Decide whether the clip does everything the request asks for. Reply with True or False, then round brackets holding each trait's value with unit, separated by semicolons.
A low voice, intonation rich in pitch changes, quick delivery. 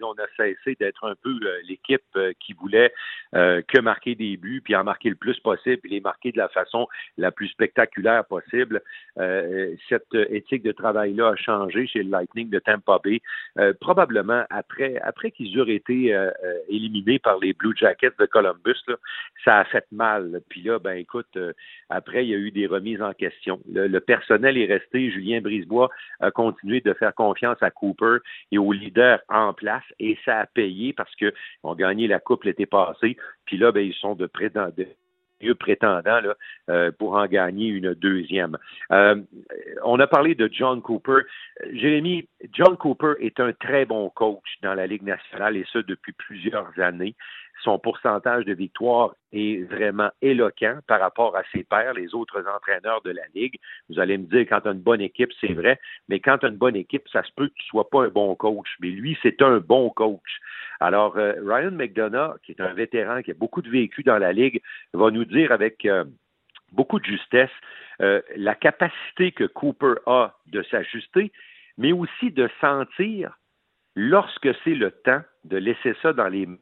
False (115 Hz; 8.4 semitones; 195 wpm)